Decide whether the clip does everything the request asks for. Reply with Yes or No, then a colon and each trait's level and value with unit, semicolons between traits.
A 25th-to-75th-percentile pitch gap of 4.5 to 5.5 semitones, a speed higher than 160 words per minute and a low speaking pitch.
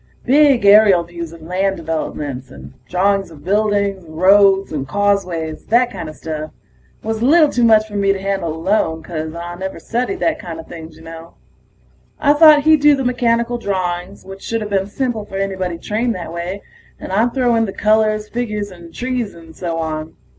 No: average, 5.0 semitones; average, 185 wpm; high, 195 Hz